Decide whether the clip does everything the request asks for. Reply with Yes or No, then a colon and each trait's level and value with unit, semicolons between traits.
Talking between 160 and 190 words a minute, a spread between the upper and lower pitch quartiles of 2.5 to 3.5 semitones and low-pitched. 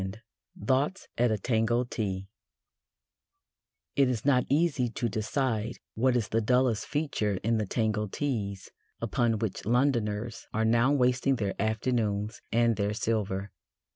No: average, 140 wpm; average, 3.1 semitones; low, 115 Hz